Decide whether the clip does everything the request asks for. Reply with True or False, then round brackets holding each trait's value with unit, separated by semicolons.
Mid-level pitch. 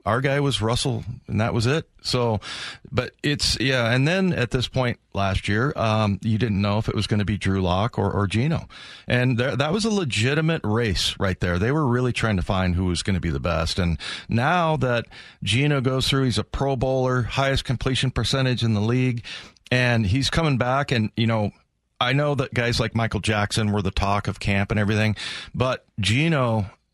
False (115 Hz)